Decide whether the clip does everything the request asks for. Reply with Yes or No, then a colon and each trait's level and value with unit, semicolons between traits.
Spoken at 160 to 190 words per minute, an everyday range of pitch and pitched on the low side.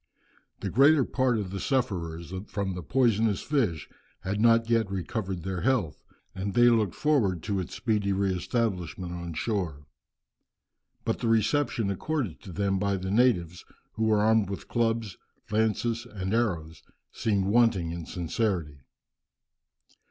No: average, 145 wpm; average, 4.1 semitones; low, 100 Hz